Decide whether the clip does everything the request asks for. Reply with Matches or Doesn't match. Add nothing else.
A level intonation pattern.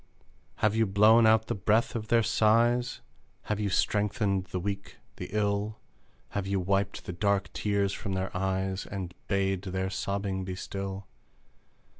Matches